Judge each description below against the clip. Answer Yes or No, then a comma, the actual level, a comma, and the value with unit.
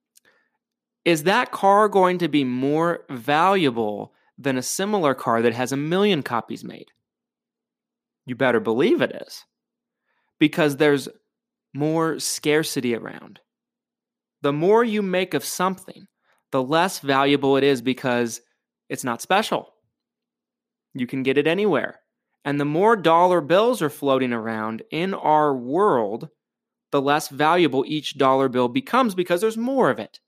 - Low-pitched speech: No, medium, 165 Hz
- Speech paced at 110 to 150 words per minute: Yes, average, 140 wpm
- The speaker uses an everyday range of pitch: No, wide, 8.6 semitones